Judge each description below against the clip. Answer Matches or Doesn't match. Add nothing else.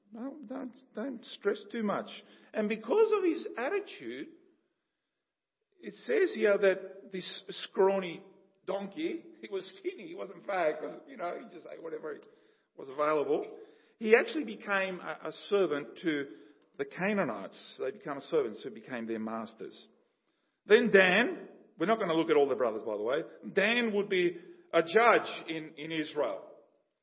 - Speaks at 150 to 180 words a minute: Matches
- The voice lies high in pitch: Matches